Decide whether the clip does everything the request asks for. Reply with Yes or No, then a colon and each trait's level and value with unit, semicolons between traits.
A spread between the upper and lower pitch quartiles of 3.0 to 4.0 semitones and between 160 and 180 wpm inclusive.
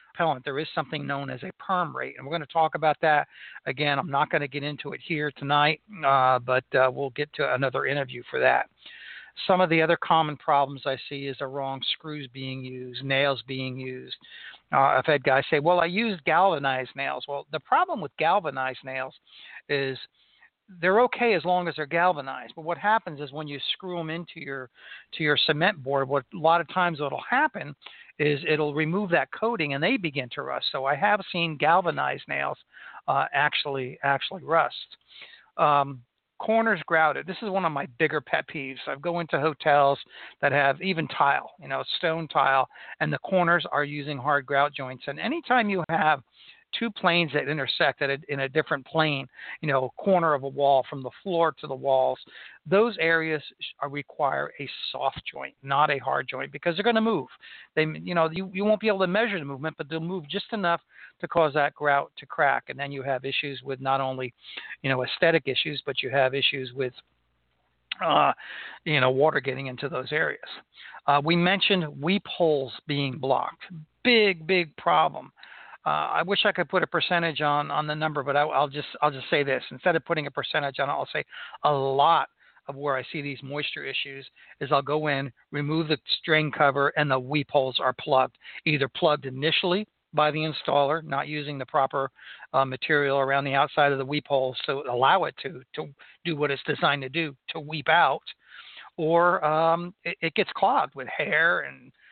No: average, 3.6 semitones; average, 200 wpm